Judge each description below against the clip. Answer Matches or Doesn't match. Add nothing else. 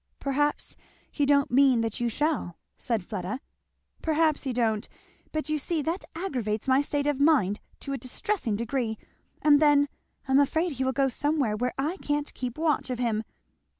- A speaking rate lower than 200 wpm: Matches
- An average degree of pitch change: Matches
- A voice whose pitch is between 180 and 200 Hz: Doesn't match